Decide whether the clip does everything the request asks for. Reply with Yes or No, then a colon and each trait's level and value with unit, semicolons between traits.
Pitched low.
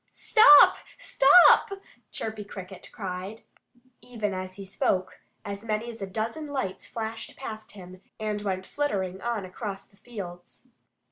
No: high, 210 Hz